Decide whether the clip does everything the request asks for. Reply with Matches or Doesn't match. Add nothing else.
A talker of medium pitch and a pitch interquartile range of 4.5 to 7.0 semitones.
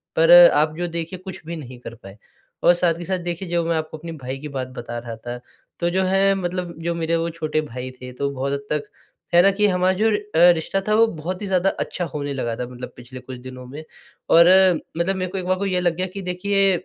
Matches